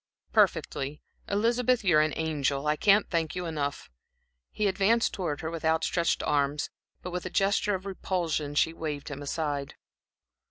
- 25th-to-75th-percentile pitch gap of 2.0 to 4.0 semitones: No, average, 4.6 semitones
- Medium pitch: Yes, medium, 160 Hz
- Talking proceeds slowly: No, average, 160 wpm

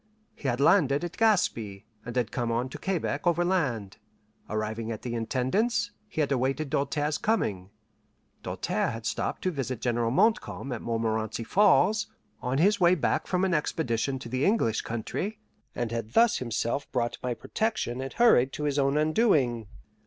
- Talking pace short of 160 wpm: No, average, 165 wpm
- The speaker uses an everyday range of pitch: No, wide, 6.9 semitones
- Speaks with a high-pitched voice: No, low, 135 Hz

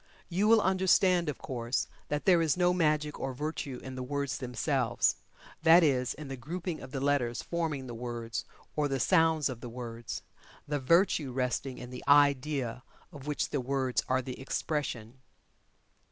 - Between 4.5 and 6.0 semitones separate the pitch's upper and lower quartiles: No, average, 3.8 semitones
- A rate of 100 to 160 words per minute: No, average, 170 wpm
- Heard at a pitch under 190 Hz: Yes, medium, 140 Hz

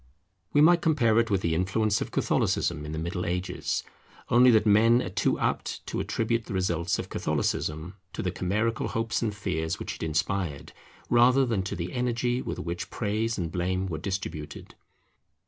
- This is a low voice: Yes, low, 100 Hz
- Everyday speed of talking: Yes, average, 180 wpm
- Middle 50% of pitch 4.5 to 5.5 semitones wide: Yes, average, 4.8 semitones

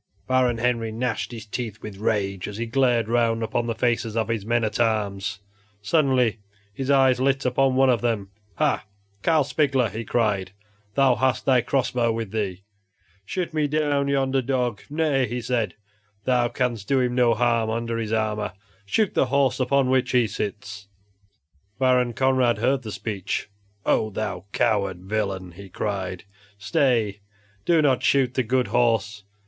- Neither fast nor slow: Yes, average, 165 wpm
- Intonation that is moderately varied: Yes, average, 3.5 semitones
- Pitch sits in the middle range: No, low, 120 Hz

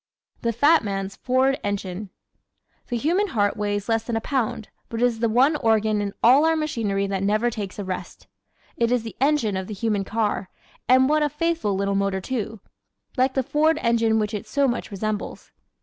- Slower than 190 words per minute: No, average, 200 wpm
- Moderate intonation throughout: Yes, average, 4.3 semitones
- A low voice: No, high, 225 Hz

